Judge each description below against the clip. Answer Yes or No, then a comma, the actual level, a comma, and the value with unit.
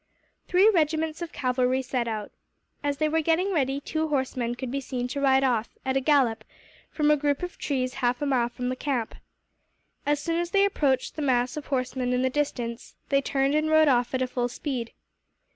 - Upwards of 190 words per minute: Yes, fast, 205 wpm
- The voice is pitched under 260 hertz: No, very high, 270 Hz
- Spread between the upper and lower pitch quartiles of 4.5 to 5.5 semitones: No, average, 3.3 semitones